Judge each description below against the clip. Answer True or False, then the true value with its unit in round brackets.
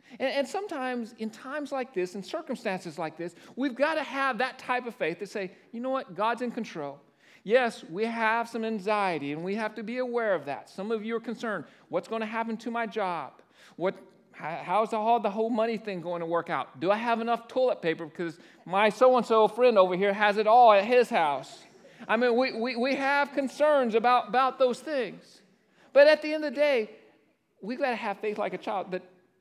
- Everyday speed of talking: False (220 wpm)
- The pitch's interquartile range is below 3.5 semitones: False (4.4 semitones)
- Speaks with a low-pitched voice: False (225 Hz)